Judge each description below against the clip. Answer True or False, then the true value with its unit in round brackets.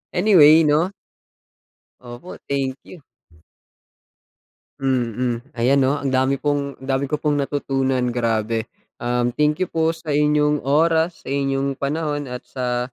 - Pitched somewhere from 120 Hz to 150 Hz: True (140 Hz)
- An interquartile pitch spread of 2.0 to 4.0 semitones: True (2.9 semitones)